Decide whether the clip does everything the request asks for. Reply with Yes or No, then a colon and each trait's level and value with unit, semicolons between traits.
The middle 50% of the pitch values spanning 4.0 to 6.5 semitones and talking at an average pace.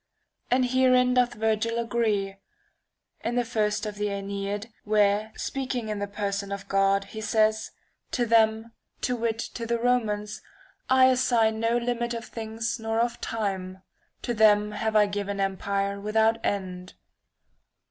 No: narrow, 2.6 semitones; average, 150 wpm